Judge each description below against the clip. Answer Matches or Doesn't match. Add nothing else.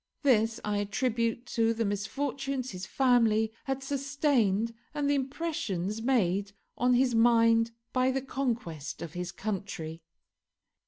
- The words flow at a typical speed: Doesn't match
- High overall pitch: Matches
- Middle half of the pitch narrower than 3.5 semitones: Doesn't match